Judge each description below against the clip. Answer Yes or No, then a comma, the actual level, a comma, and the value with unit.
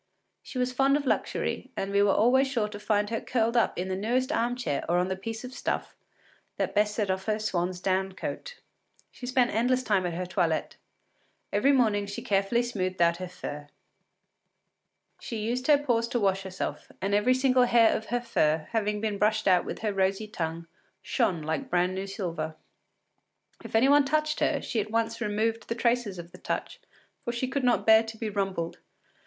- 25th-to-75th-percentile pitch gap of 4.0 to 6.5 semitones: Yes, average, 4.3 semitones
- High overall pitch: Yes, high, 215 Hz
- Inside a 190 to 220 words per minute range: Yes, average, 200 wpm